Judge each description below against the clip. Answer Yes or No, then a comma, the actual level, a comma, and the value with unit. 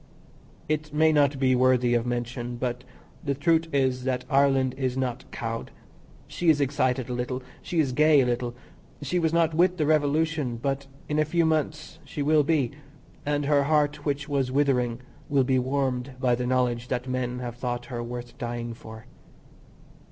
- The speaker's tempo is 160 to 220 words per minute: Yes, average, 180 wpm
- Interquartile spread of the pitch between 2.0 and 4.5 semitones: Yes, average, 3.2 semitones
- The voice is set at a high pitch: No, low, 130 Hz